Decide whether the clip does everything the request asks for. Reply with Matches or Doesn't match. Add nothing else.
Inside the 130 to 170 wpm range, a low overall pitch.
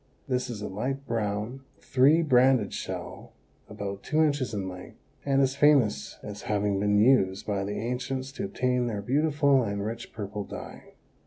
Matches